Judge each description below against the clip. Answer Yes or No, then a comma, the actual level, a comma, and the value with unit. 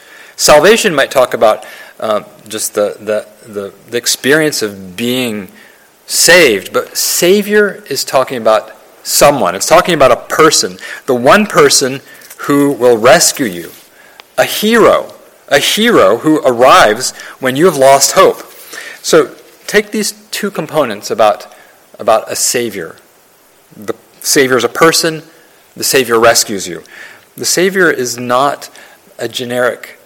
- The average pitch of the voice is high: No, medium, 140 Hz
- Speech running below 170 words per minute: Yes, slow, 135 wpm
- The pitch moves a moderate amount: No, wide, 7.5 semitones